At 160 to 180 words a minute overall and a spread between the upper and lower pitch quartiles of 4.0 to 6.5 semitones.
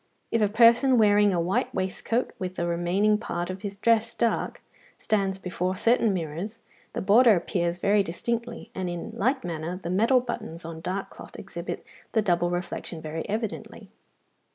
Yes: average, 165 wpm; average, 4.4 semitones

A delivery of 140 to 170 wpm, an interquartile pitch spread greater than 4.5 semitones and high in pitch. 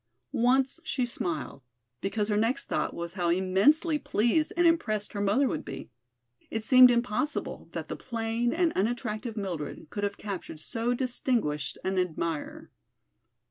Yes: average, 145 wpm; average, 5.2 semitones; high, 215 Hz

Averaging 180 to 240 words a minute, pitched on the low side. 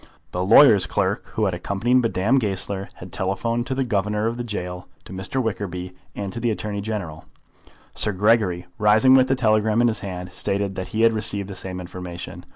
Yes: average, 195 wpm; low, 105 Hz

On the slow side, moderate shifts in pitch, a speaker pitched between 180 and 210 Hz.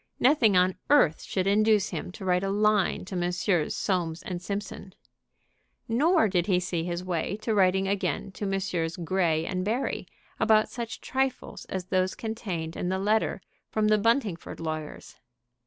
No: average, 160 wpm; average, 3.2 semitones; high, 190 Hz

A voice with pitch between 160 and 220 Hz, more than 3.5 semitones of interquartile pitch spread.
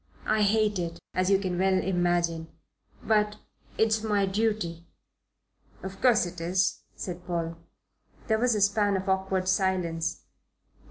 No: high, 190 Hz; average, 3.0 semitones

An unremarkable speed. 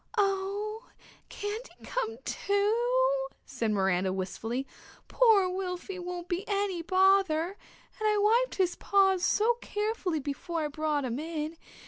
No: slow, 130 wpm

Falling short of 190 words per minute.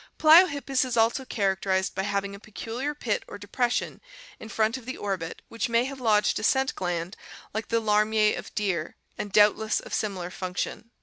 No: average, 195 wpm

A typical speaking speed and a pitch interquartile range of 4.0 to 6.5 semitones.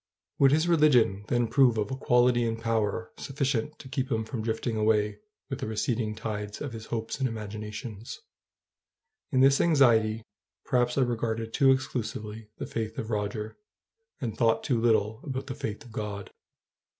No: average, 165 wpm; average, 3.1 semitones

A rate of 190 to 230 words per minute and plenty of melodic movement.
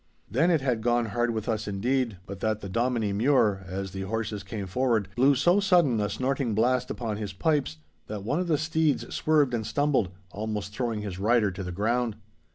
No: average, 200 wpm; average, 4.4 semitones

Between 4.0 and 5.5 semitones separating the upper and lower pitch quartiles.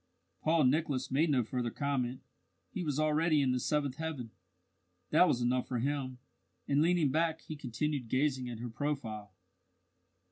No: average, 3.4 semitones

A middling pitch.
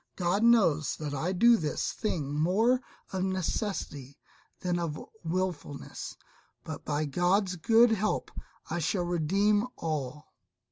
Yes: medium, 175 Hz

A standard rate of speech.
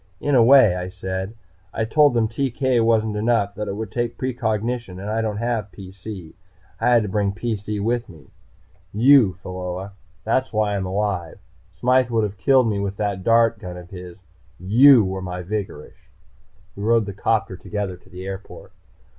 Yes: average, 180 wpm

